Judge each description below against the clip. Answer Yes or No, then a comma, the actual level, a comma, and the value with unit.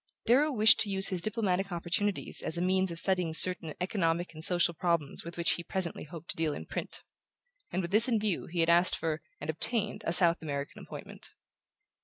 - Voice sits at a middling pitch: Yes, medium, 175 Hz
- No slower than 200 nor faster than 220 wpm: Yes, fast, 205 wpm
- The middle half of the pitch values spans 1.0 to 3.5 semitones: Yes, average, 2.8 semitones